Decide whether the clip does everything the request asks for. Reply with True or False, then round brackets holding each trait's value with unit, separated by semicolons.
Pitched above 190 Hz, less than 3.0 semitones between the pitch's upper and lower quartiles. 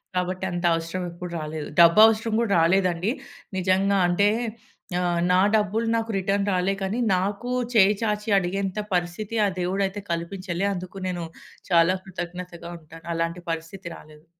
False (185 Hz; 2.6 semitones)